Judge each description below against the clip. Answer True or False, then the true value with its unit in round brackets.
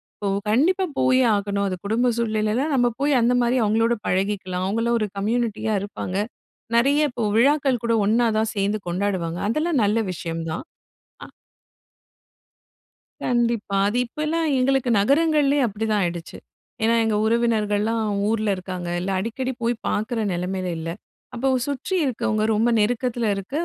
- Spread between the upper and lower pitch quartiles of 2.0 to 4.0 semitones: True (3.5 semitones)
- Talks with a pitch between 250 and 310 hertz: False (225 Hz)